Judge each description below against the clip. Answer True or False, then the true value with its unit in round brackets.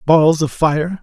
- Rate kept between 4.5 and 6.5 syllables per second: False (3.3 syllables/s)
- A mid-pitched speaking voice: True (155 Hz)